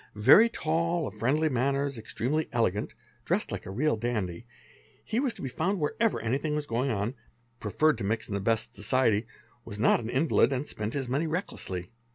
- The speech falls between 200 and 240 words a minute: Yes, fast, 205 wpm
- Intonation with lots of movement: Yes, wide, 5.9 semitones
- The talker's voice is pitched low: Yes, low, 130 Hz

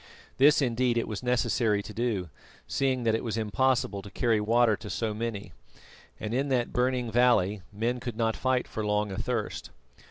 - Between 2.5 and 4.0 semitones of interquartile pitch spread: Yes, average, 2.8 semitones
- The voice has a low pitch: Yes, low, 115 Hz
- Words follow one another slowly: No, average, 180 wpm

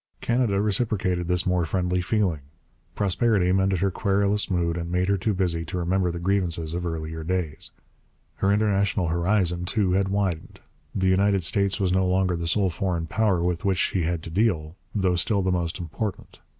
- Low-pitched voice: Yes, very low, 90 Hz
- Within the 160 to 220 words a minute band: Yes, average, 180 wpm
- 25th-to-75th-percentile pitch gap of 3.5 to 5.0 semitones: No, narrow, 2.4 semitones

